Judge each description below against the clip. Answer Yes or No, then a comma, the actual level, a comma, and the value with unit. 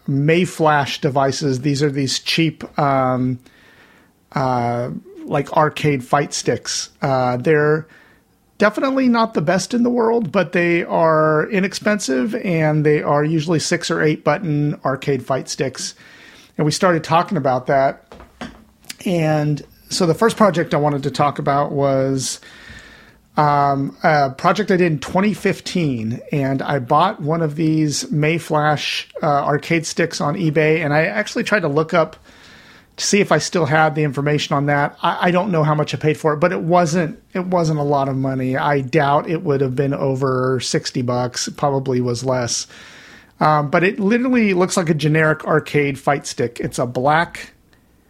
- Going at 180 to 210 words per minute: No, average, 170 wpm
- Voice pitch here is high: No, medium, 155 Hz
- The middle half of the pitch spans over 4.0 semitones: No, average, 3.7 semitones